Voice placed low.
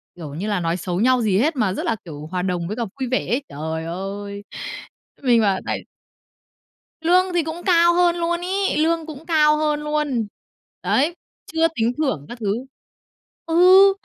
No: very high, 255 Hz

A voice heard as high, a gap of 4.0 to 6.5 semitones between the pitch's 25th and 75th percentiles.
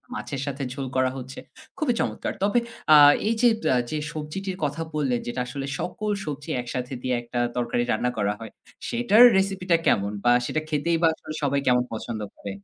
No: medium, 140 Hz; wide, 5.5 semitones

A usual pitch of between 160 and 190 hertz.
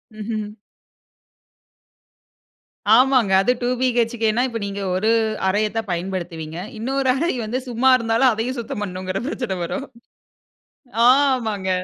No: high, 225 Hz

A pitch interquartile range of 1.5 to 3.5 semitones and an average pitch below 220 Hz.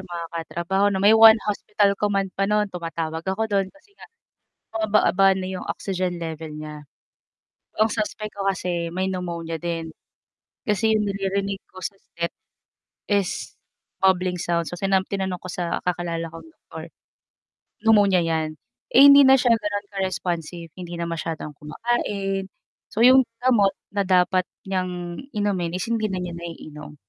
Yes: average, 3.0 semitones; medium, 185 Hz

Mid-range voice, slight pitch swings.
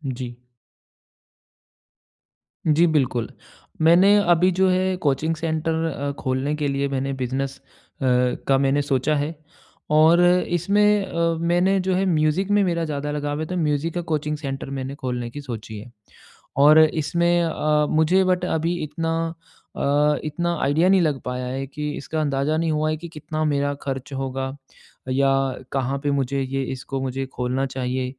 No: medium, 150 Hz; average, 3.6 semitones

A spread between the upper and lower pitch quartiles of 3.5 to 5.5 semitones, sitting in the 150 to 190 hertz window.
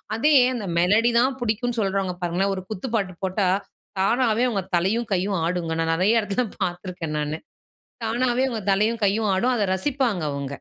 No: average, 4.4 semitones; high, 200 Hz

